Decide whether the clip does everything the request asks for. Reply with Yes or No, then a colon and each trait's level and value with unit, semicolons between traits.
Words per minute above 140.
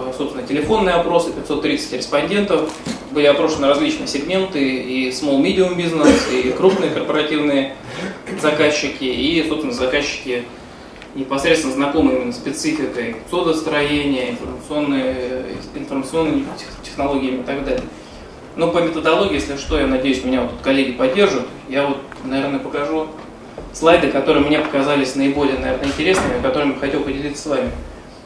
No: average, 125 wpm